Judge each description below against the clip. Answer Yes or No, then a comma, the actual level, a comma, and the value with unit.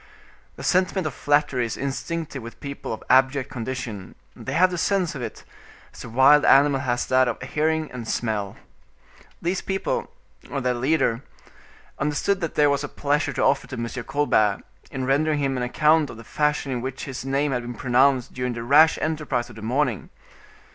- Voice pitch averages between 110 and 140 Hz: Yes, low, 135 Hz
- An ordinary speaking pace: Yes, average, 190 wpm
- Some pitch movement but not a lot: Yes, average, 3.4 semitones